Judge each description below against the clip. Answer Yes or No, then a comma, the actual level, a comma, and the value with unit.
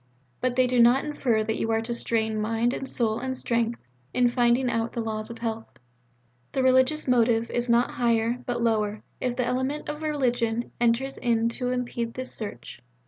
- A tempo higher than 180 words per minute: Yes, average, 190 wpm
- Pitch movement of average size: No, narrow, 1.9 semitones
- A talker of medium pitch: No, high, 240 Hz